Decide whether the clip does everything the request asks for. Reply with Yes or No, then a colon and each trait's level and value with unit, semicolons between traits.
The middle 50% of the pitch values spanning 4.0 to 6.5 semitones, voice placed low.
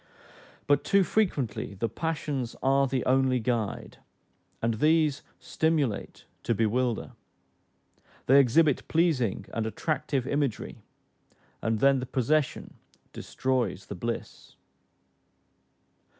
Yes: average, 4.5 semitones; low, 130 Hz